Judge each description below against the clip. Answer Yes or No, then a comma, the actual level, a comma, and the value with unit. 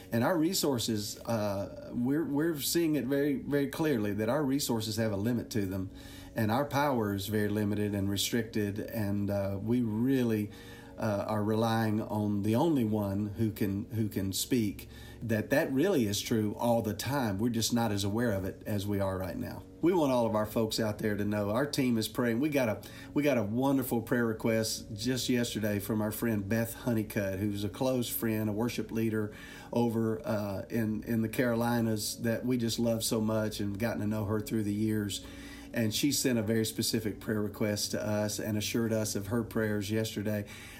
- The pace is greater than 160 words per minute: Yes, average, 200 wpm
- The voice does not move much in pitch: Yes, narrow, 2.1 semitones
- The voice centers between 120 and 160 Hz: No, low, 110 Hz